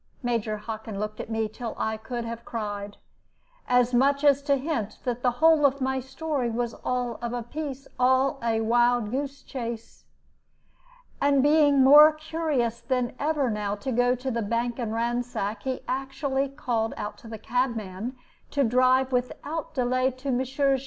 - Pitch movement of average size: Yes, average, 3.0 semitones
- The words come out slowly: No, average, 165 wpm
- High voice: Yes, very high, 250 Hz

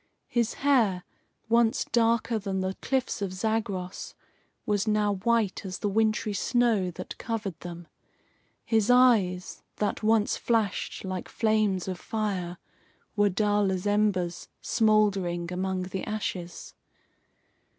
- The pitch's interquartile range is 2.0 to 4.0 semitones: Yes, average, 3.2 semitones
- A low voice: No, high, 205 Hz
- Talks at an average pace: No, slow, 120 wpm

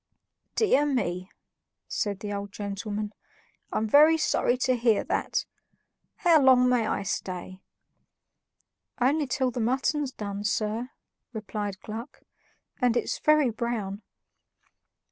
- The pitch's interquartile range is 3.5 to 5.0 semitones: Yes, average, 4.1 semitones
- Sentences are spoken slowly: Yes, slow, 115 wpm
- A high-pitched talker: Yes, high, 230 Hz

